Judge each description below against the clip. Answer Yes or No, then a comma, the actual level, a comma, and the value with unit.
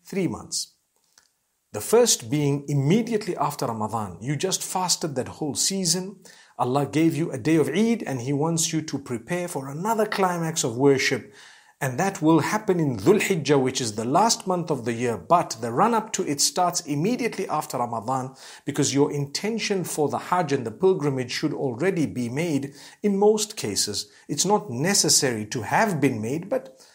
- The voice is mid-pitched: Yes, medium, 150 Hz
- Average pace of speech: Yes, average, 180 wpm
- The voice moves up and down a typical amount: No, wide, 5.7 semitones